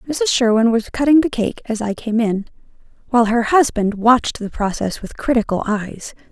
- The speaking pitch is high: Yes, high, 230 Hz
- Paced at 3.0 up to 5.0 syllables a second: No, 5.2 syllables/s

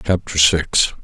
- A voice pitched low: Yes, very low, 85 Hz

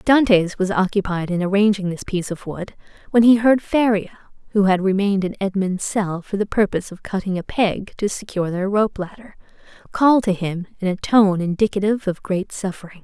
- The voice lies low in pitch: No, high, 195 Hz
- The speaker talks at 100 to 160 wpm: No, average, 190 wpm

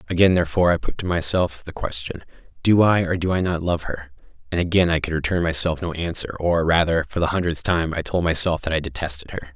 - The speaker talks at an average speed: No, fast, 230 wpm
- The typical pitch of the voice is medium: No, very low, 85 Hz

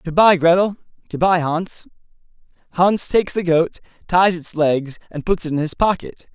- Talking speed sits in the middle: Yes, average, 160 wpm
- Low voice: No, medium, 170 Hz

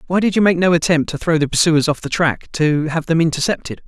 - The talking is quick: Yes, fast, 265 wpm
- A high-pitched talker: No, medium, 160 Hz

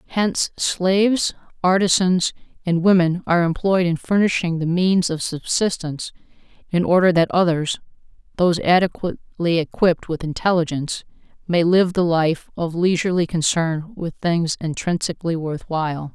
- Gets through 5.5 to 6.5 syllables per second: No, 5.0 syllables/s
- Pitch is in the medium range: Yes, medium, 175 Hz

